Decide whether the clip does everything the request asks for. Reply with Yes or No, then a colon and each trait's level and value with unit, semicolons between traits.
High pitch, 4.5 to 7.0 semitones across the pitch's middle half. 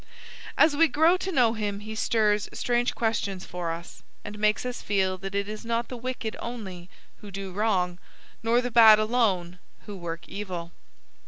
No: high, 210 Hz; average, 3.7 semitones